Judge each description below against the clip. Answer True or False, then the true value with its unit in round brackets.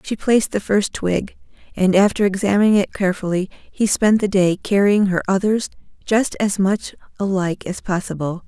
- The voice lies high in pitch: True (195 Hz)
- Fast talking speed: False (165 wpm)